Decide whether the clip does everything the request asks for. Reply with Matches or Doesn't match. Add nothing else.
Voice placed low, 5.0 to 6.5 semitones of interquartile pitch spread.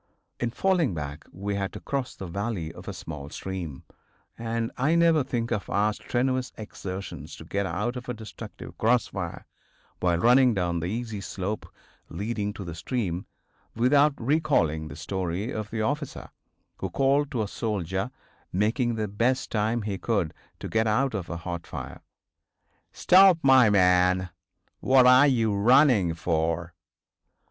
Matches